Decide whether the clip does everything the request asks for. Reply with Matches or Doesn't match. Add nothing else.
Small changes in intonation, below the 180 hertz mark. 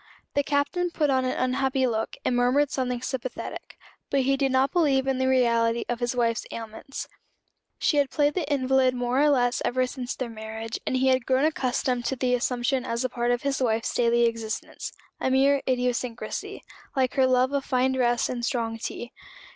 Doesn't match